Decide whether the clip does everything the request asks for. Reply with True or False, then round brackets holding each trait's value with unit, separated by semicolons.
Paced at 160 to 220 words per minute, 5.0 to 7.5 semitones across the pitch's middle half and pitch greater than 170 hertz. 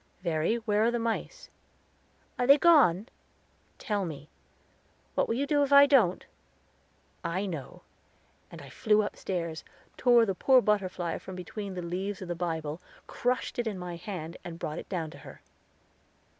True (165 wpm; 5.4 semitones; 190 Hz)